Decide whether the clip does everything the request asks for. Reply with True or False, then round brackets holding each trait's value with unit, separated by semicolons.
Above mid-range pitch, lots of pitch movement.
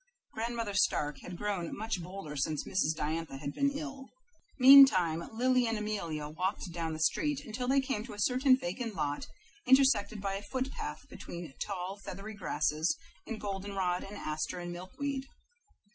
True (200 Hz; 6.6 semitones)